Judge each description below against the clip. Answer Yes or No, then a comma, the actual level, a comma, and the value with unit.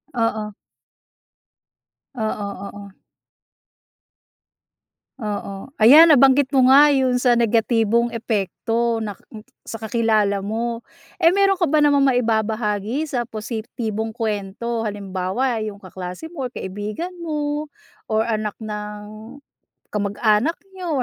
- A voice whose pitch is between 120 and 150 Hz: No, high, 225 Hz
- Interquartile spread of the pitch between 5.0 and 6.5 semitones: No, average, 3.8 semitones